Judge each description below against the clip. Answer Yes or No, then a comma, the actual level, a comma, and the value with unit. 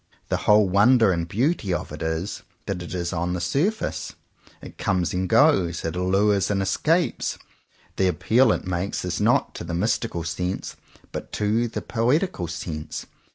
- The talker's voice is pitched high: No, very low, 95 Hz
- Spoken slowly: No, average, 165 wpm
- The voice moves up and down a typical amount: Yes, average, 4.6 semitones